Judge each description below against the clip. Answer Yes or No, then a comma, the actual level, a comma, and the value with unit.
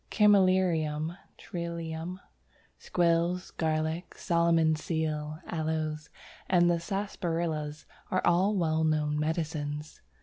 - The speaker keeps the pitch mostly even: Yes, narrow, 1.9 semitones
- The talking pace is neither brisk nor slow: No, slow, 90 wpm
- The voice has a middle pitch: Yes, medium, 165 Hz